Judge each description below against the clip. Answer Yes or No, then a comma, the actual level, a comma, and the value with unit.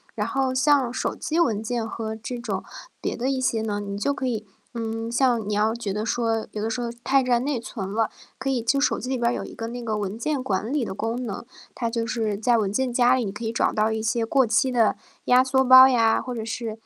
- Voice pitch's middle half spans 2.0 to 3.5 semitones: Yes, average, 2.7 semitones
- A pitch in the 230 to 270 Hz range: Yes, high, 235 Hz